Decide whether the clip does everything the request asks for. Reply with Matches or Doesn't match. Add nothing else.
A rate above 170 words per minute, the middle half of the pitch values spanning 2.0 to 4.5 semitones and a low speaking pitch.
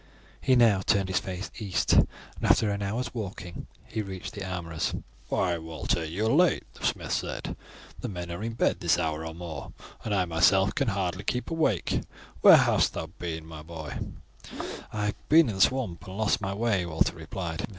Matches